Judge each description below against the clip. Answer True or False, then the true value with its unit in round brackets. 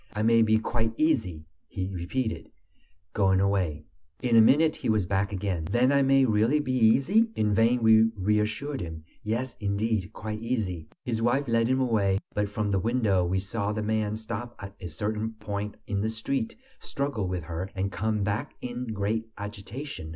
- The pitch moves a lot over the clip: False (3.2 semitones)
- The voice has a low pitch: True (110 Hz)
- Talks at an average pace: True (180 wpm)